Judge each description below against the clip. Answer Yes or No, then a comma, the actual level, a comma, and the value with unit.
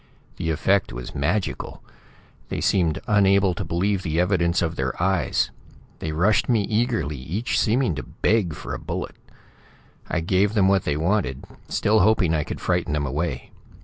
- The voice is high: No, very low, 90 Hz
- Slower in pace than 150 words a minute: No, average, 165 wpm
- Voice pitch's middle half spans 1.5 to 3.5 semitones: No, average, 4.6 semitones